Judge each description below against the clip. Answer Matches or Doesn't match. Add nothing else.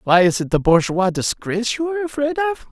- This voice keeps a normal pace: Doesn't match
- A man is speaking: Matches